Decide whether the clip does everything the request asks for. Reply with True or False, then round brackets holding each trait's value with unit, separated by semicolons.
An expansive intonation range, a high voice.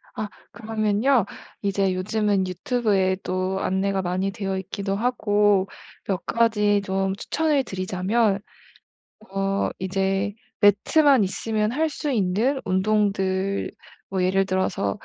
False (2.2 semitones; 195 Hz)